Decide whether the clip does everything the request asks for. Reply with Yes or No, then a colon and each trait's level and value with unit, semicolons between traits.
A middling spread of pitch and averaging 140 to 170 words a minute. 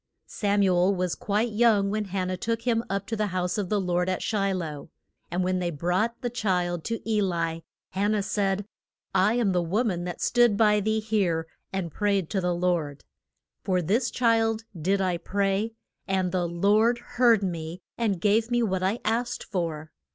No: average, 3.4 semitones; average, 195 wpm